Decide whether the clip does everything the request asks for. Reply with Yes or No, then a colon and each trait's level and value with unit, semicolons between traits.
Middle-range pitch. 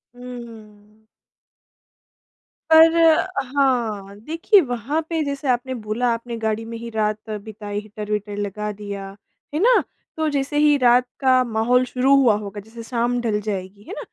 No: high, 230 Hz